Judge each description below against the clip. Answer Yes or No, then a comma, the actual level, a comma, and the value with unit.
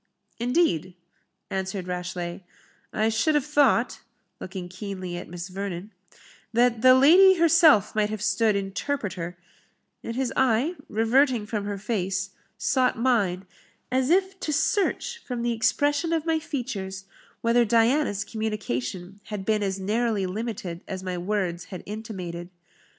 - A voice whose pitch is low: No, high, 215 Hz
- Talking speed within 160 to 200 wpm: No, slow, 135 wpm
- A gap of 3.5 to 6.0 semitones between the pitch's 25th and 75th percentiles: Yes, average, 5.2 semitones